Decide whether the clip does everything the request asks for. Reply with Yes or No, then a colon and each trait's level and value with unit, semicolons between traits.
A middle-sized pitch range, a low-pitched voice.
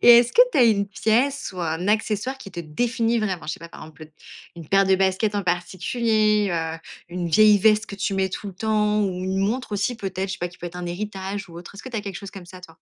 No: average, 3.2 semitones; high, 195 Hz